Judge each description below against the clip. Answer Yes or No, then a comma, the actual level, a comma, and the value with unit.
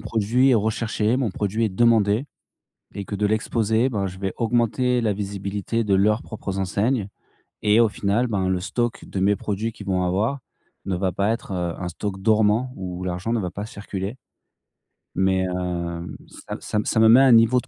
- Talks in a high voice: No, low, 105 Hz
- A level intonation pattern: No, average, 3.1 semitones